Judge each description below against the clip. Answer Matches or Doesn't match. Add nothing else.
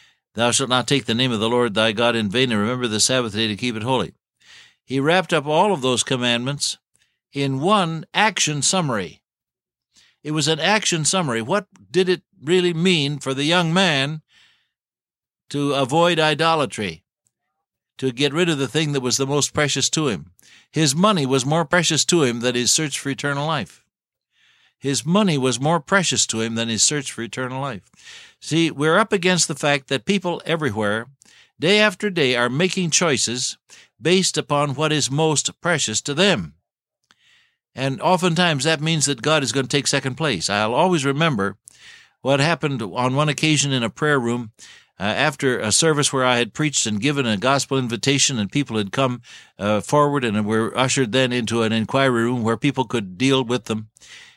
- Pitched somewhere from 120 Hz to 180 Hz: Matches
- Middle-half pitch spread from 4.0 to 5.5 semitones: Matches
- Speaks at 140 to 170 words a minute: Doesn't match